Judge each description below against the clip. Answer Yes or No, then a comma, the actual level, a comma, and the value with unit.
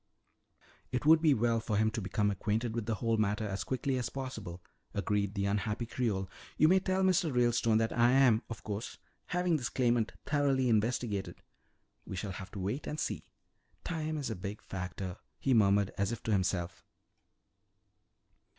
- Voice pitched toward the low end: Yes, low, 115 Hz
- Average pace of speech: Yes, average, 175 wpm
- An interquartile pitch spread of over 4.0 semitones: Yes, average, 4.4 semitones